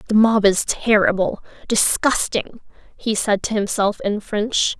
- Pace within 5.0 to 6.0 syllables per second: No, 4.0 syllables/s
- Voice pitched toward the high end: Yes, high, 215 Hz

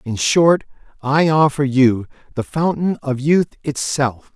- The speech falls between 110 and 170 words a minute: Yes, average, 140 wpm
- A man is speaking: Yes, male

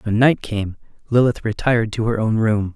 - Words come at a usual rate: Yes, average, 195 wpm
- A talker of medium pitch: No, low, 110 Hz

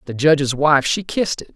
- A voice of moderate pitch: Yes, medium, 150 Hz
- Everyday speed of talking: No, fast, 230 wpm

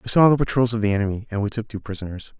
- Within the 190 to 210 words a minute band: No, fast, 300 wpm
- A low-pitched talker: Yes, low, 110 Hz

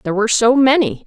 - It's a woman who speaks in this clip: Yes, female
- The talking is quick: Yes, fast, 225 wpm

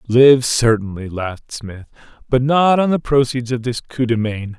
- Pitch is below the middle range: Yes, low, 120 Hz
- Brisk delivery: No, average, 185 wpm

